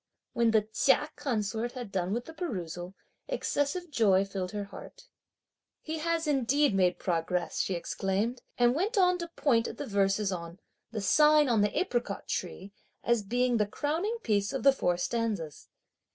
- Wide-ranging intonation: Yes, wide, 6.9 semitones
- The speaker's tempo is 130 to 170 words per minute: Yes, average, 165 wpm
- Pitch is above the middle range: Yes, high, 230 Hz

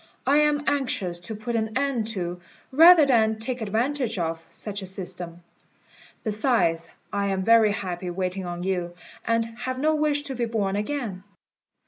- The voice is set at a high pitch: Yes, high, 220 Hz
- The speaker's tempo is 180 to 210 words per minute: No, average, 160 wpm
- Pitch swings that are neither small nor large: No, wide, 5.7 semitones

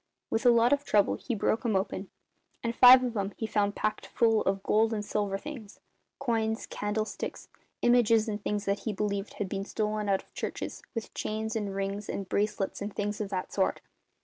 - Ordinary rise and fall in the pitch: No, narrow, 2.0 semitones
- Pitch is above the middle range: Yes, high, 210 Hz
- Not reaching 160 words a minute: No, average, 200 wpm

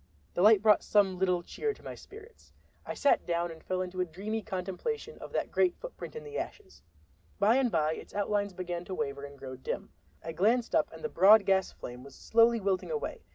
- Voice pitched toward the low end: No, high, 195 Hz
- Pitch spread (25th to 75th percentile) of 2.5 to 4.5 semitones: No, average, 5.1 semitones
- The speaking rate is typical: No, fast, 215 wpm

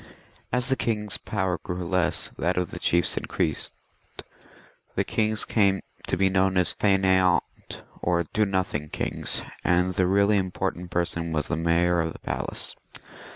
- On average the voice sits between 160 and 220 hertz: No, very low, 90 Hz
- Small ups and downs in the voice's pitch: Yes, narrow, 2.0 semitones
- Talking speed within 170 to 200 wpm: No, average, 155 wpm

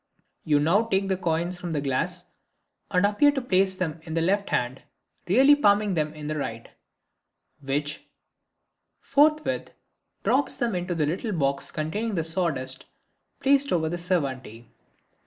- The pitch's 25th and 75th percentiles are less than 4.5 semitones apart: No, average, 5.3 semitones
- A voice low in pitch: No, medium, 175 Hz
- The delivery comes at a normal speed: Yes, average, 145 wpm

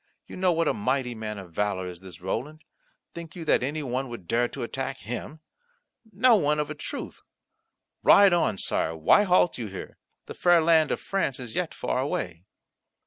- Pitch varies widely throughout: Yes, wide, 8.0 semitones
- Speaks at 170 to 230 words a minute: Yes, average, 195 wpm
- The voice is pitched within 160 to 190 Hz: No, low, 135 Hz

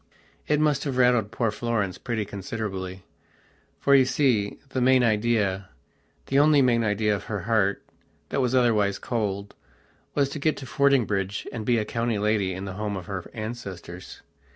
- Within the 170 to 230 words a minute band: No, average, 160 wpm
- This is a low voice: Yes, low, 110 Hz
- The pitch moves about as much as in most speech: Yes, average, 3.9 semitones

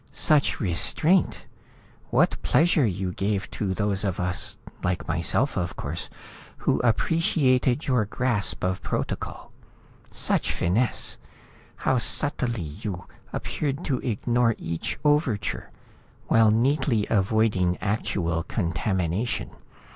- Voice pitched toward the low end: Yes, low, 105 Hz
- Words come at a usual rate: No, slow, 105 wpm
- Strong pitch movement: Yes, wide, 5.8 semitones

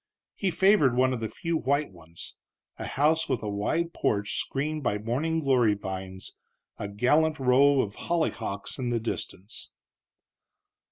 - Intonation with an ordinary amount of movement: No, wide, 7.0 semitones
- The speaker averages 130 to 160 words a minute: Yes, average, 150 wpm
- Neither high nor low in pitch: No, low, 130 Hz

